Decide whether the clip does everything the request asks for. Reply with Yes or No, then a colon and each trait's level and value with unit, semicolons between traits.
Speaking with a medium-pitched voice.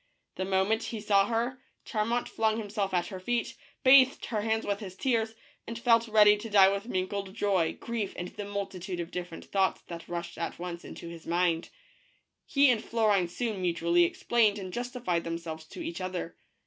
No: high, 200 Hz